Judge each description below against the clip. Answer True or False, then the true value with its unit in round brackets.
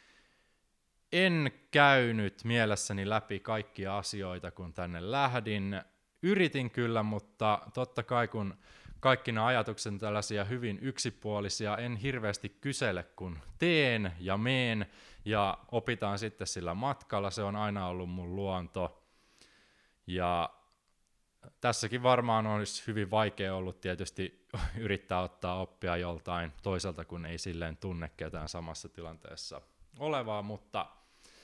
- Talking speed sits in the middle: True (115 wpm)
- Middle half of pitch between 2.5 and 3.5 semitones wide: False (4.5 semitones)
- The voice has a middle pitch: False (105 Hz)